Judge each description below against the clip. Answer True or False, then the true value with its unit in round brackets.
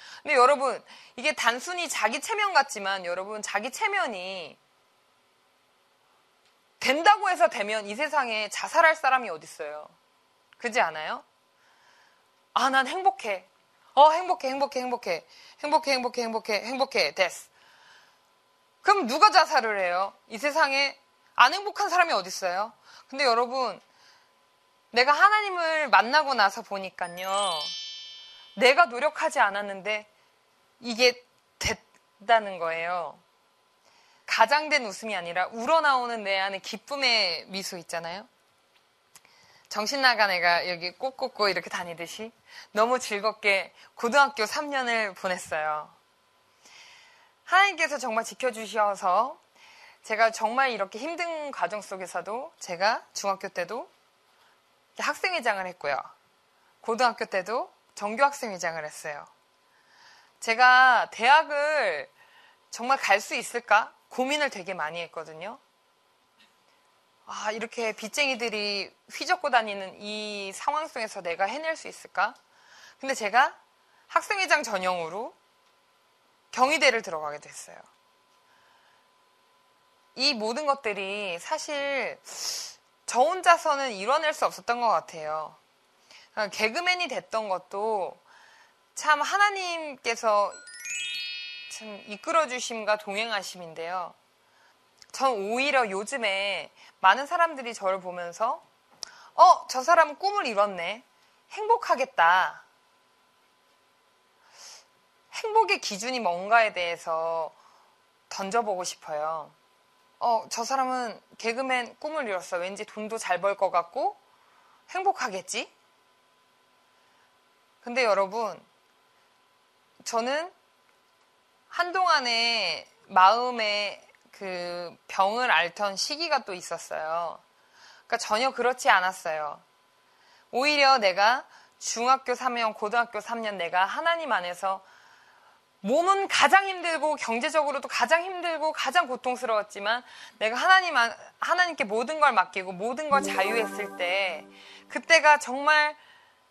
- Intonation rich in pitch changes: True (7.4 semitones)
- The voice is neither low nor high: False (235 Hz)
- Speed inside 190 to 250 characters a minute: True (240 characters per minute)